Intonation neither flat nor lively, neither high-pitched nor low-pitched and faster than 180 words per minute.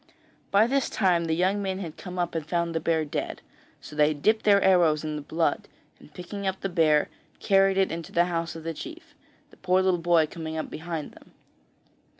Yes: average, 3.1 semitones; medium, 175 Hz; fast, 205 wpm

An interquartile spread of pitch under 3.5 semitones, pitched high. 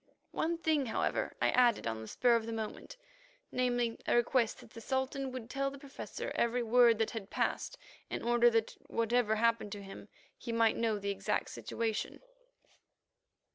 Yes: average, 2.8 semitones; high, 235 Hz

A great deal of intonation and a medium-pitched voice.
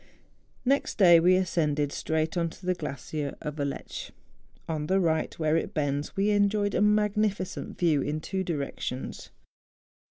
No: average, 4.4 semitones; medium, 165 Hz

